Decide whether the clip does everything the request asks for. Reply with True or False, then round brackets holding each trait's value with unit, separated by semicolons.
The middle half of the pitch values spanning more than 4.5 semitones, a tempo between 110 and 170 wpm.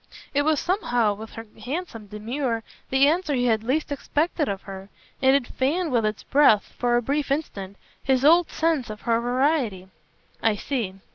False (4.9 semitones; 180 wpm)